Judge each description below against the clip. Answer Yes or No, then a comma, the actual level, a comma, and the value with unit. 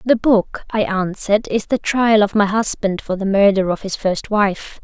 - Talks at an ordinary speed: No, fast, 210 wpm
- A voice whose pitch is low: No, high, 205 Hz